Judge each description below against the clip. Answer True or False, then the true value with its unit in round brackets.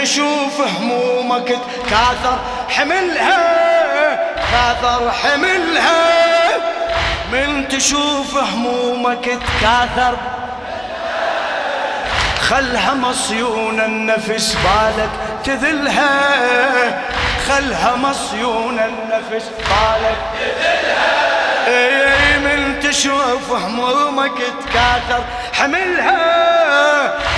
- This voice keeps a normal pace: False (55 wpm)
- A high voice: True (255 Hz)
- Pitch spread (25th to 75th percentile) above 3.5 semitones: False (2.9 semitones)